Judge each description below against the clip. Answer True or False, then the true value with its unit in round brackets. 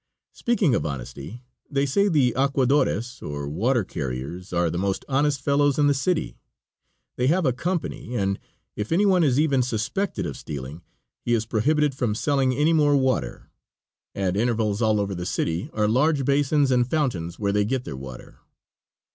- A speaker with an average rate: True (170 wpm)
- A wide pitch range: True (6.6 semitones)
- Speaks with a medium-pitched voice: False (125 Hz)